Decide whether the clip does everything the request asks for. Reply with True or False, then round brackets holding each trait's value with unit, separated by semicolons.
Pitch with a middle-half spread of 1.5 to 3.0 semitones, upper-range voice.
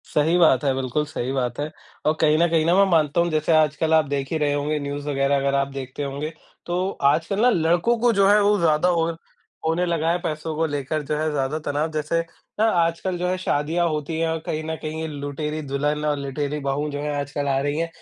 False (2.5 semitones; 155 Hz)